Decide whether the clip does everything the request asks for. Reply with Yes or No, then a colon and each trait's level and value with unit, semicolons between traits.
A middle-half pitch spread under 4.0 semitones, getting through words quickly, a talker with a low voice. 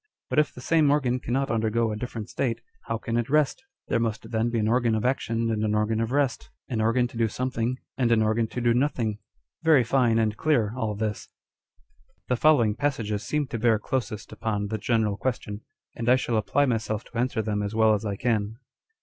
Yes: narrow, 2.6 semitones; fast, 215 wpm; low, 115 Hz